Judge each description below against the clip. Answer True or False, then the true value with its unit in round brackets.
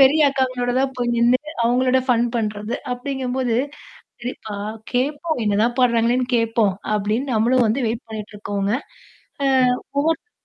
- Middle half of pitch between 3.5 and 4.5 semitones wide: False (2.6 semitones)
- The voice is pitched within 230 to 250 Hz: True (245 Hz)